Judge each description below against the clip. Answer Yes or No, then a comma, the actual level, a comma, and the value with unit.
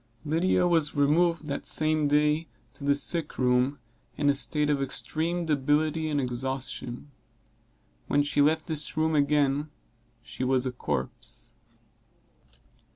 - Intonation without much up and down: Yes, narrow, 2.3 semitones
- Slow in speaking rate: Yes, slow, 130 wpm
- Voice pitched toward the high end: No, medium, 145 Hz